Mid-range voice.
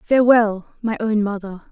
No: high, 215 Hz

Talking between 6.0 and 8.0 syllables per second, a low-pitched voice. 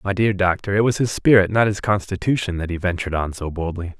Yes: 6.2 syllables/s; very low, 95 Hz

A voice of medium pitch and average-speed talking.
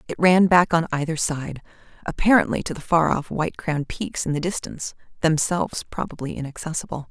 Yes: medium, 165 Hz; average, 170 wpm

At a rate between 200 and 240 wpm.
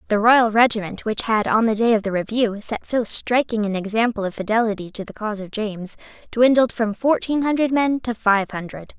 Yes: fast, 205 wpm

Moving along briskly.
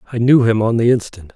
Yes: fast, 265 wpm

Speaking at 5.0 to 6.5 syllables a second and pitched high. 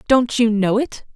No: 4.4 syllables/s; high, 230 Hz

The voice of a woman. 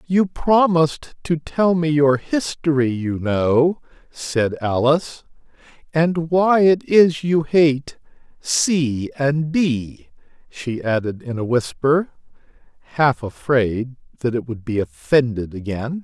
No: male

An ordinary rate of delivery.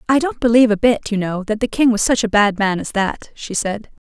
No: fast, 280 wpm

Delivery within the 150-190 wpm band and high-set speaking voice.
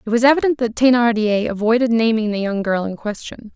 No: average, 200 wpm; high, 225 Hz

